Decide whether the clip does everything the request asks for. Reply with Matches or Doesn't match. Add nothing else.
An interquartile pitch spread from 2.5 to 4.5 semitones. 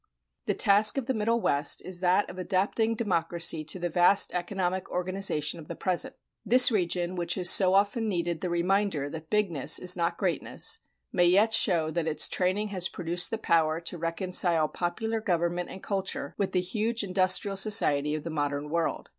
Matches